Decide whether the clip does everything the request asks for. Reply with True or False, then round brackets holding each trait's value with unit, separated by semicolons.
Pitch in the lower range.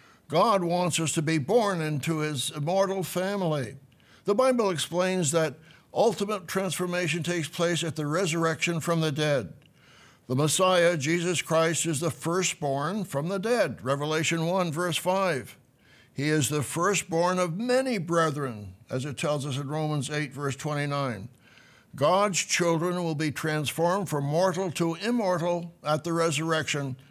False (165 Hz)